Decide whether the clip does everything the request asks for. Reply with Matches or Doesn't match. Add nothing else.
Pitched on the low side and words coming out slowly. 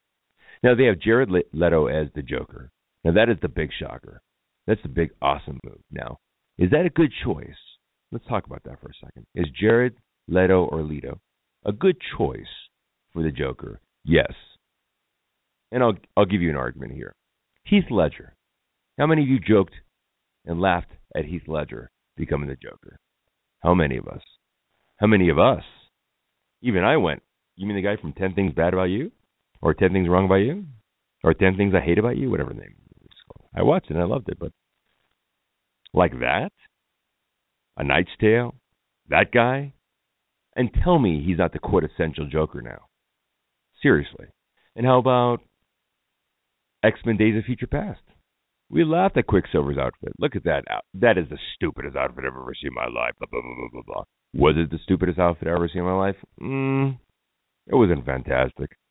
Doesn't match